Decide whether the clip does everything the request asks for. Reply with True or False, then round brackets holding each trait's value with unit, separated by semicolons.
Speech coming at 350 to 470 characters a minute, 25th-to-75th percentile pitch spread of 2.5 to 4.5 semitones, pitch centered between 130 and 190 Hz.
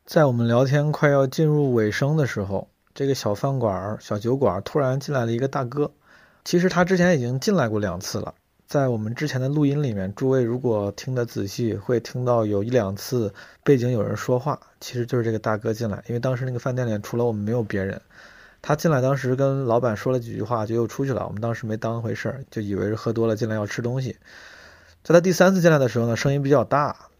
False (355 characters per minute; 4.0 semitones; 120 Hz)